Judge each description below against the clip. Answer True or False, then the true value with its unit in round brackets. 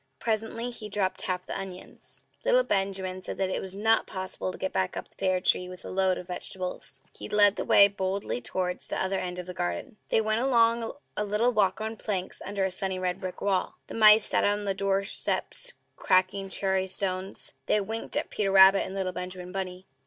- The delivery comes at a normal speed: False (210 wpm)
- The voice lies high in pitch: True (195 Hz)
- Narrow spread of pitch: True (2.2 semitones)